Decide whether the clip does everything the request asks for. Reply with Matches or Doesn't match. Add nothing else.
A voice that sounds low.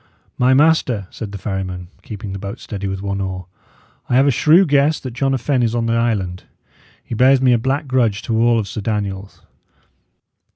Matches